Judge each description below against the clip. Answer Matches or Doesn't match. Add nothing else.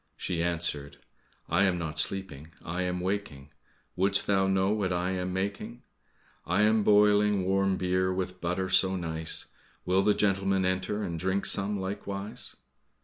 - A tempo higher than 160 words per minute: Doesn't match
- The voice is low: Matches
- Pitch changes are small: Matches